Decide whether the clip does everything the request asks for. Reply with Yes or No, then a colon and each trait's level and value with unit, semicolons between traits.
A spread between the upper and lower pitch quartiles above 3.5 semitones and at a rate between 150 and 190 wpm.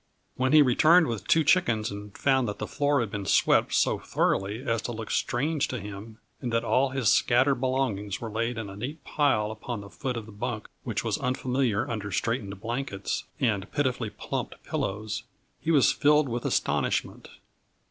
Yes: average, 4.1 semitones; average, 185 wpm